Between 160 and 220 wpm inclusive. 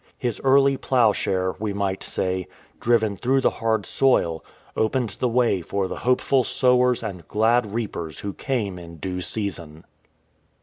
No: average, 145 wpm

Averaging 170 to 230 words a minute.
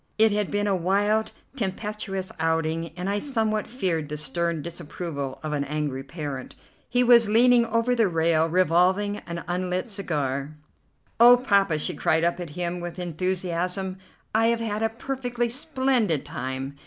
No: average, 155 wpm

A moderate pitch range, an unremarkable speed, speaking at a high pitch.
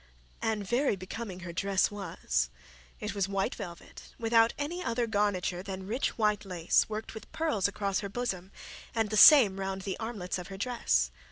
Yes: average, 3.3 semitones; average, 175 wpm; high, 200 Hz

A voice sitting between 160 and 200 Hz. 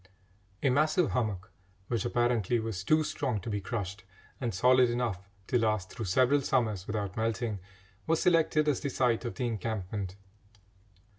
No: low, 115 Hz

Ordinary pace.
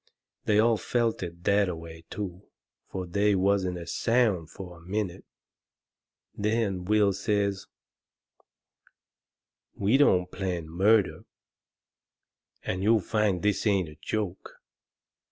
No: slow, 120 wpm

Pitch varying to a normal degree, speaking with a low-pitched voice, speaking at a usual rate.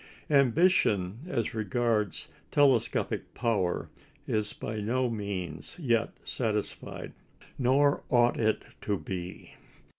No: average, 3.8 semitones; low, 110 Hz; slow, 95 wpm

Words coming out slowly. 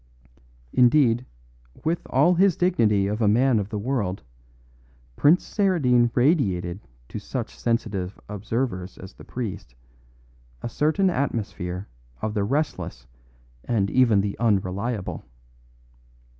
Yes: slow, 115 wpm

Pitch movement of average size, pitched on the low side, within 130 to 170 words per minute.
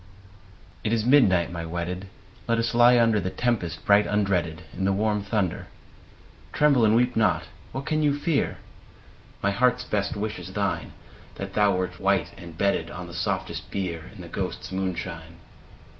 No: average, 4.1 semitones; low, 100 Hz; average, 180 wpm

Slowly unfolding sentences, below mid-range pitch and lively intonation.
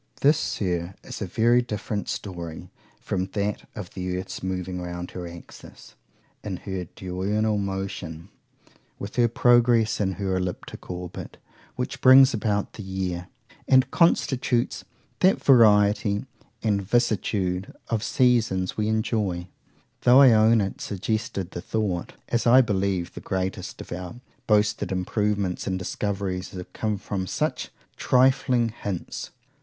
No: slow, 130 wpm; low, 100 Hz; average, 3.6 semitones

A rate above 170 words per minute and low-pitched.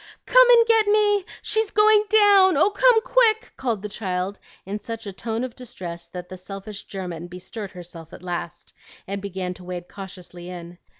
No: average, 180 wpm; high, 200 Hz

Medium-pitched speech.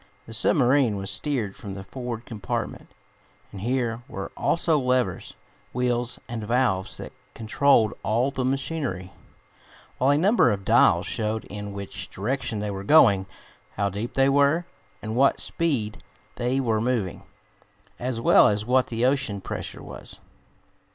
No: low, 115 Hz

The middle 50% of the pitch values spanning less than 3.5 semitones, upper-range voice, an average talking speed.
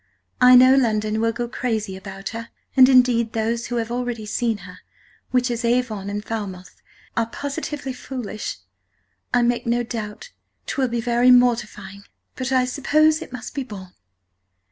Yes: average, 2.8 semitones; high, 235 Hz; average, 160 wpm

